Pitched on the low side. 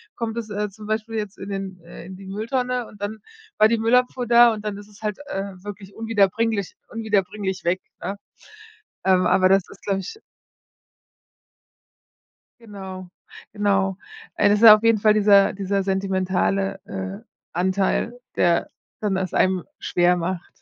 No: high, 200 Hz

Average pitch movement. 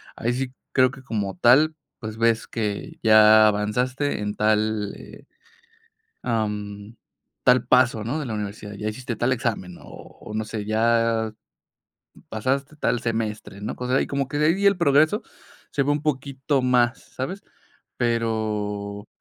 Yes: average, 3.5 semitones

